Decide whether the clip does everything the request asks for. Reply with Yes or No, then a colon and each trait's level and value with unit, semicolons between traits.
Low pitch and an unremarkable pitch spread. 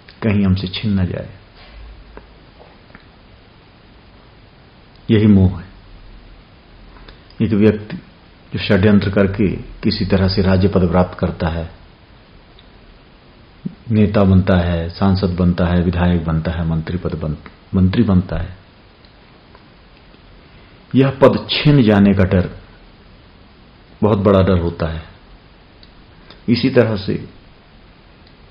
Yes: very low, 95 Hz; average, 3.1 semitones